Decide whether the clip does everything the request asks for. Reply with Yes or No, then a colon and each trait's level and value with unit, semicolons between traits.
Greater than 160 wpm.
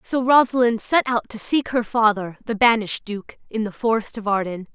Yes: average, 200 wpm